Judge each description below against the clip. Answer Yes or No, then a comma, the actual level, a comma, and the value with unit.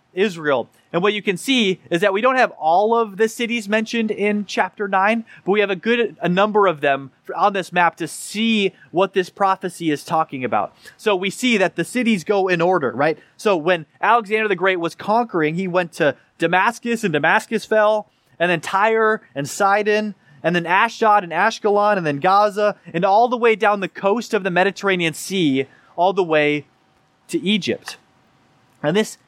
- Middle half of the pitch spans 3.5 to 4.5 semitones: Yes, average, 4.1 semitones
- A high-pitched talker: Yes, high, 195 Hz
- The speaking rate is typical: Yes, average, 195 wpm